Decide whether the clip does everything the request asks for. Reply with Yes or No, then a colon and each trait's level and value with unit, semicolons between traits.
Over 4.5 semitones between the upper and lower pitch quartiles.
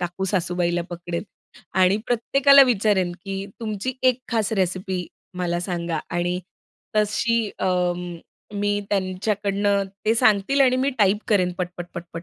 No: average, 3.2 semitones